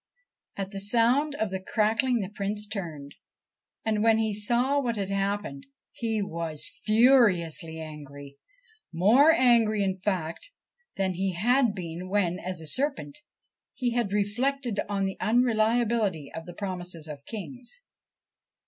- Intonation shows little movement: No, average, 4.7 semitones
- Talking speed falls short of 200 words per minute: Yes, average, 140 wpm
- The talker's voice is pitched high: Yes, high, 205 Hz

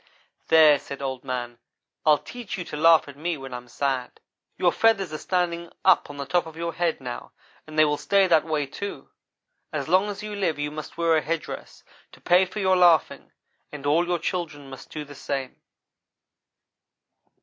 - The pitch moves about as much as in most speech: Yes, average, 3.8 semitones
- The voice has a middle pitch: Yes, medium, 155 Hz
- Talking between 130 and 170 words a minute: No, average, 195 wpm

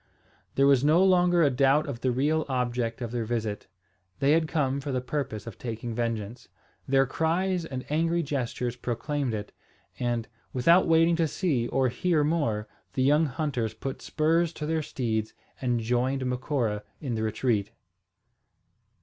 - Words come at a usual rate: Yes, average, 160 wpm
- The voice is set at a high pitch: No, low, 130 Hz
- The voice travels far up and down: No, average, 4.5 semitones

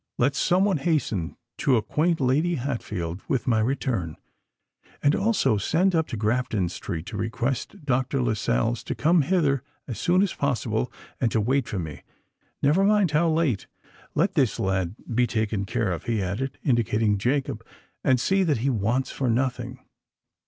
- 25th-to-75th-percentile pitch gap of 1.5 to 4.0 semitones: No, average, 5.2 semitones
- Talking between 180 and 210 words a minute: No, average, 160 wpm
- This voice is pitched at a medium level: No, low, 125 Hz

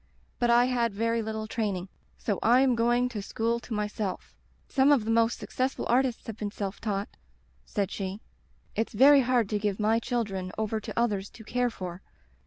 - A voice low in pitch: No, high, 225 Hz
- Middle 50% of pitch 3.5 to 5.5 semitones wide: No, average, 2.7 semitones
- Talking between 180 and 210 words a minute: Yes, average, 195 wpm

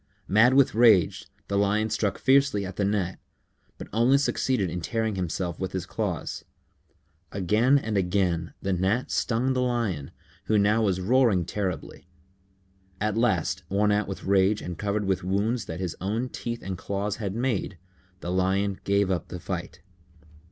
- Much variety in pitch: No, average, 3.2 semitones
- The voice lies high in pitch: No, low, 100 Hz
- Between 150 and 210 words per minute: Yes, average, 165 wpm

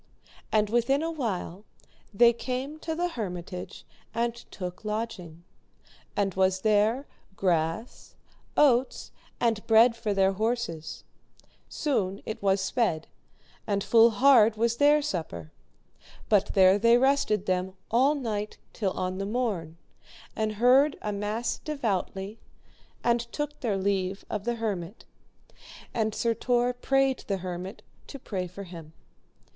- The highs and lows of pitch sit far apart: No, average, 4.0 semitones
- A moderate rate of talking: No, slow, 130 wpm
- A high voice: Yes, high, 215 Hz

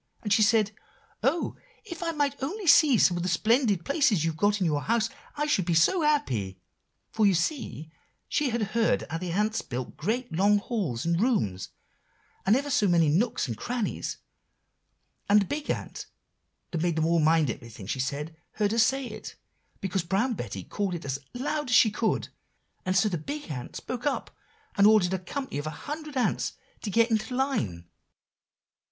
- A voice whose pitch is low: No, high, 205 Hz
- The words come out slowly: No, average, 190 wpm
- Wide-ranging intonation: Yes, wide, 7.4 semitones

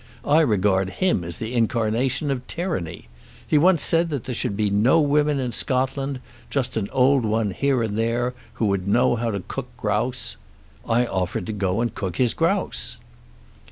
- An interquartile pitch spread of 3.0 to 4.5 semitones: No, average, 5.0 semitones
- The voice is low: Yes, low, 120 Hz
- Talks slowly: No, average, 175 wpm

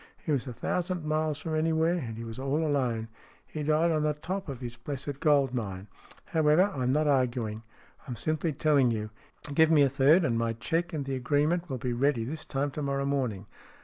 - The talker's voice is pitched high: No, medium, 140 Hz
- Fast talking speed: Yes, fast, 210 wpm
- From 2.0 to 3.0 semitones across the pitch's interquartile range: No, average, 3.9 semitones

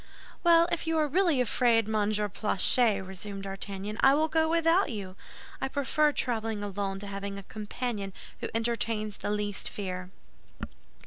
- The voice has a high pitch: Yes, high, 215 Hz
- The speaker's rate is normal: Yes, average, 150 wpm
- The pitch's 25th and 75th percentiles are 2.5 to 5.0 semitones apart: No, wide, 5.4 semitones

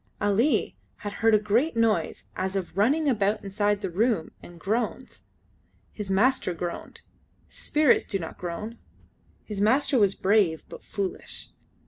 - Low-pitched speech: No, high, 205 Hz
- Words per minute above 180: No, average, 140 wpm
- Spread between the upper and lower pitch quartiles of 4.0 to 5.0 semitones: No, average, 3.0 semitones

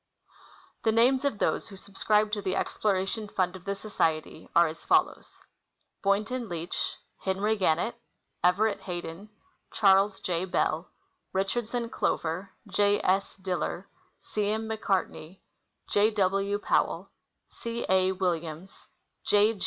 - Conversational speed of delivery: No, slow, 125 wpm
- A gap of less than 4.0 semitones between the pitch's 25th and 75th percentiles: Yes, narrow, 2.5 semitones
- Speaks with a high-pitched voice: Yes, high, 195 Hz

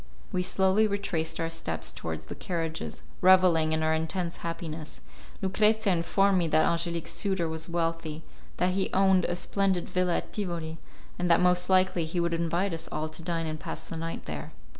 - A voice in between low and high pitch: Yes, medium, 170 Hz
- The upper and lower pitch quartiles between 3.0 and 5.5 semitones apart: No, narrow, 2.5 semitones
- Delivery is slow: No, average, 180 wpm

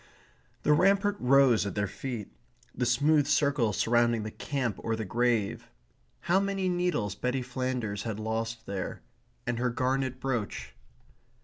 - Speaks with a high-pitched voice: No, low, 125 Hz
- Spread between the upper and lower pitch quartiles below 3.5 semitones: No, average, 3.9 semitones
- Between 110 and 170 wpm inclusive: Yes, average, 140 wpm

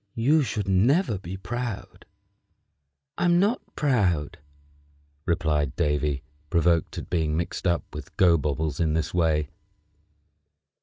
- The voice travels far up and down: Yes, wide, 6.6 semitones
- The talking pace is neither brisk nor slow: No, slow, 110 wpm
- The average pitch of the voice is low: Yes, very low, 85 Hz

